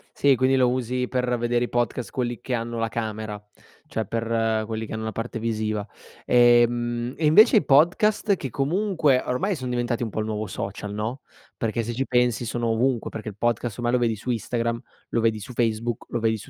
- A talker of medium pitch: No, low, 120 Hz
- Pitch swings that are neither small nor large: No, narrow, 2.1 semitones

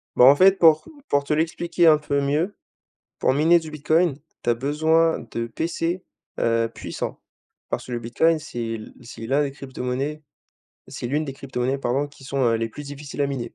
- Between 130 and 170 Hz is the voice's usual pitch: Yes, medium, 140 Hz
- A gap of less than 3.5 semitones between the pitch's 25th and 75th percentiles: No, average, 4.0 semitones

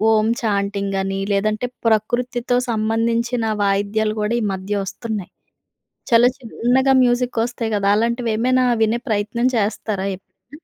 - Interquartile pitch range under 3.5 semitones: Yes, average, 2.7 semitones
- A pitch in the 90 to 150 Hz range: No, high, 225 Hz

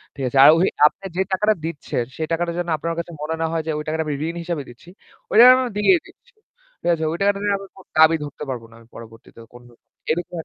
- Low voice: No, medium, 165 Hz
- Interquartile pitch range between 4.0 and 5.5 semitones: Yes, average, 4.5 semitones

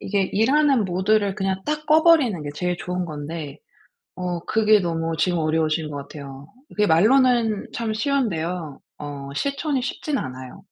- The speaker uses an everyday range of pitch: No, wide, 6.4 semitones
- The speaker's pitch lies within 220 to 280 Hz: No, medium, 185 Hz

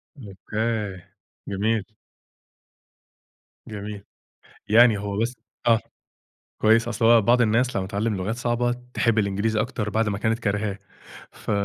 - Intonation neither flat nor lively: No, narrow, 2.2 semitones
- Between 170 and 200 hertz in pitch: No, low, 110 Hz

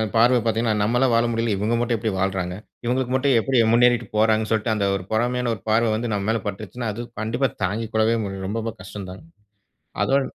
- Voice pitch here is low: Yes, low, 115 Hz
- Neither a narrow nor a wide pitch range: No, narrow, 2.2 semitones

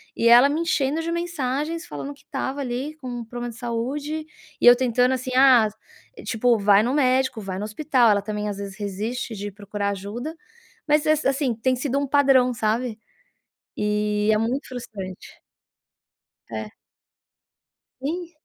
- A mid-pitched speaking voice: No, high, 245 Hz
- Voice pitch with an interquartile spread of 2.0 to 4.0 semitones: No, average, 4.7 semitones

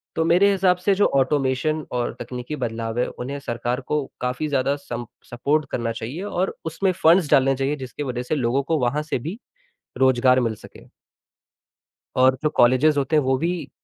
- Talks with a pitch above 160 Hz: No, low, 135 Hz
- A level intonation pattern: No, average, 3.8 semitones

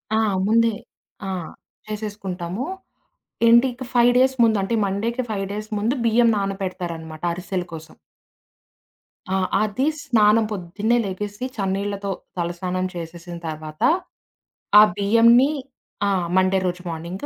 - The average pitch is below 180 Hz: No, high, 200 Hz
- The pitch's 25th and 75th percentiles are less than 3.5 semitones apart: No, average, 4.1 semitones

